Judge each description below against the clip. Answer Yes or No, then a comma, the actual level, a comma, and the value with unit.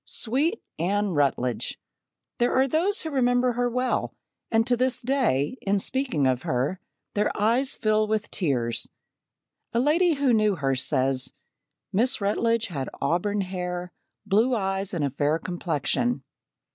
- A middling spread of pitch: No, wide, 7.5 semitones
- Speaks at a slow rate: No, average, 145 wpm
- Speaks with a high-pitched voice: Yes, high, 210 Hz